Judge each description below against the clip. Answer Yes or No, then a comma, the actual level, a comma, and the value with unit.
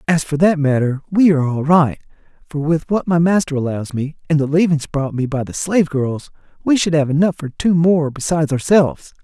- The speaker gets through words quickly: Yes, fast, 215 wpm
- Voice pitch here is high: No, medium, 155 Hz